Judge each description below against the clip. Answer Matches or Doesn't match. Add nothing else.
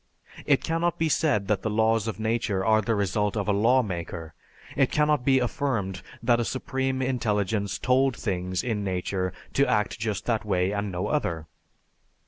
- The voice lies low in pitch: Matches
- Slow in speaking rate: Doesn't match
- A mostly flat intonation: Doesn't match